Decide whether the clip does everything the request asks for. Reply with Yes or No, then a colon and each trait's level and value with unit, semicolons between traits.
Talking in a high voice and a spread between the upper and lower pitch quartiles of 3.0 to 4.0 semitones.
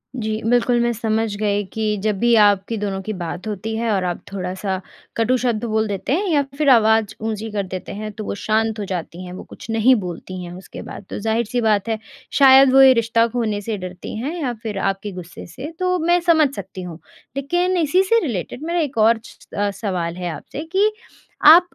No: high, 220 Hz; average, 4.5 semitones